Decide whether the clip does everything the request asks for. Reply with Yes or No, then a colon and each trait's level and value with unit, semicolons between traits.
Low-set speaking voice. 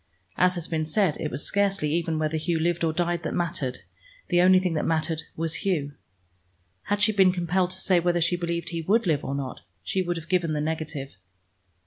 No: medium, 170 Hz